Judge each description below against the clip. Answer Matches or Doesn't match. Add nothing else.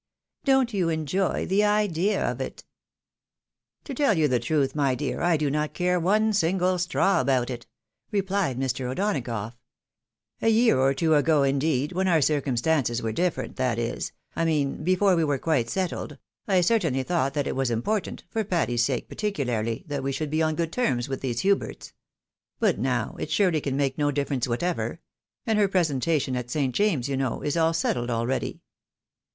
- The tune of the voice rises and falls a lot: Matches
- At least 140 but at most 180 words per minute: Doesn't match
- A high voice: Doesn't match